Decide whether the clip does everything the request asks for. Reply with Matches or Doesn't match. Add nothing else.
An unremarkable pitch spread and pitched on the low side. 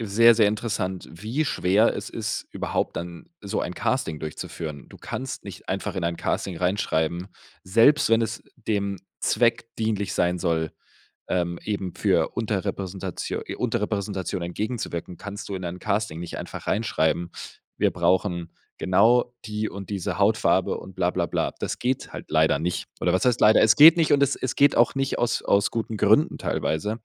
Matches